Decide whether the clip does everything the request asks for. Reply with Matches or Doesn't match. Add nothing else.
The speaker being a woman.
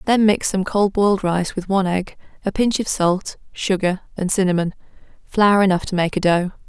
Matches